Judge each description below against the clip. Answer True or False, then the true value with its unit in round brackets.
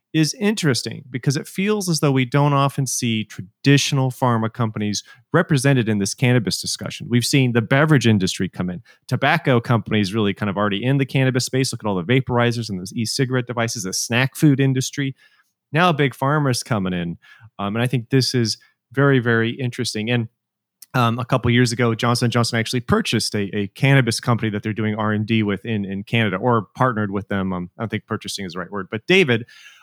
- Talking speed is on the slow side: False (205 wpm)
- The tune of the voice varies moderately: True (3.9 semitones)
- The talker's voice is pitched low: True (120 Hz)